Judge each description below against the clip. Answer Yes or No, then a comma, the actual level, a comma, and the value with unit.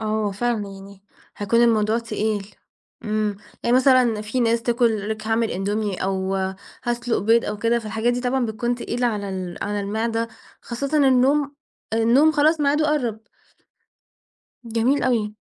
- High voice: Yes, high, 230 Hz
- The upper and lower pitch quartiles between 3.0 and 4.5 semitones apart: No, narrow, 2.6 semitones